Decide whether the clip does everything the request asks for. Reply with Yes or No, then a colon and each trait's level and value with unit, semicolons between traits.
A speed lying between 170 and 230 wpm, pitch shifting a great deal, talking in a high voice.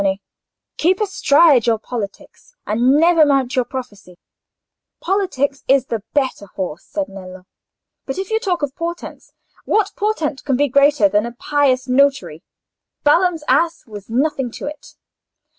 No: average, 160 wpm; wide, 6.1 semitones; very high, 275 Hz